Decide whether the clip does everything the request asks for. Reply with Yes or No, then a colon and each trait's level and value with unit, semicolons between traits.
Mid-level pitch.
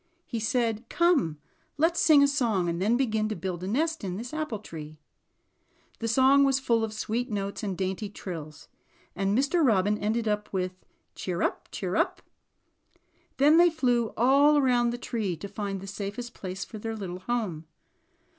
No: high, 220 Hz